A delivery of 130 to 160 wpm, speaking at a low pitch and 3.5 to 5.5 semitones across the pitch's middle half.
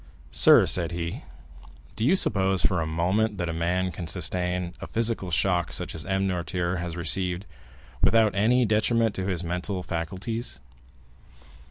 No: average, 155 wpm; very low, 90 Hz; average, 2.8 semitones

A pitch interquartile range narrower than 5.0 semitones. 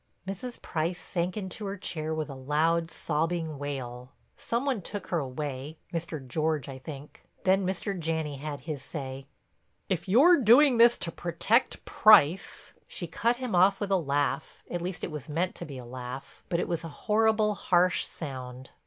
No: average, 5.3 semitones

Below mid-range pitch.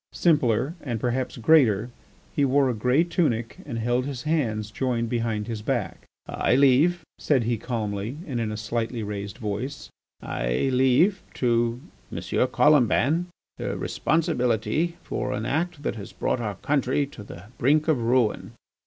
Yes: low, 125 Hz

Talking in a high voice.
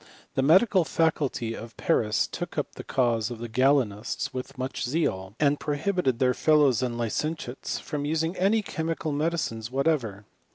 No: low, 135 Hz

